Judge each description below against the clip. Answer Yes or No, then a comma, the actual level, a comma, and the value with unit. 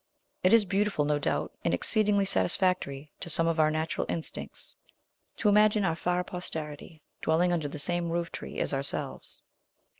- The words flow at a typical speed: Yes, average, 160 wpm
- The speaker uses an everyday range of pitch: Yes, average, 3.7 semitones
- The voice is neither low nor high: Yes, medium, 170 Hz